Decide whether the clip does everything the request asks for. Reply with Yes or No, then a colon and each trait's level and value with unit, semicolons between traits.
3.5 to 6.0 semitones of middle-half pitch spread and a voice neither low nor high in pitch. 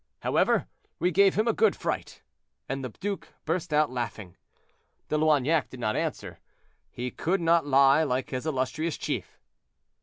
Yes: average, 4.7 semitones; medium, 150 Hz